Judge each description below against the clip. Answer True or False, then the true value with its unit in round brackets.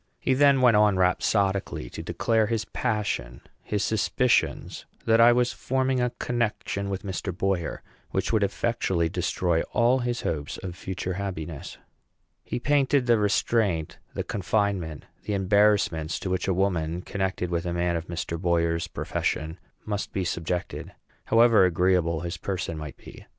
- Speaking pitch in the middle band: False (95 Hz)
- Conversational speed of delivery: True (150 wpm)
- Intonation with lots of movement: False (4.6 semitones)